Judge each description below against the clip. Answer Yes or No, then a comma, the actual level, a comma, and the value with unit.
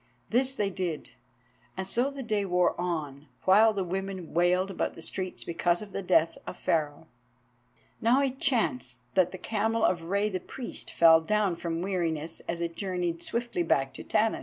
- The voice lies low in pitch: No, medium, 185 Hz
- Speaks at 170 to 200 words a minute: Yes, average, 180 wpm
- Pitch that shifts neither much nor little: Yes, average, 4.0 semitones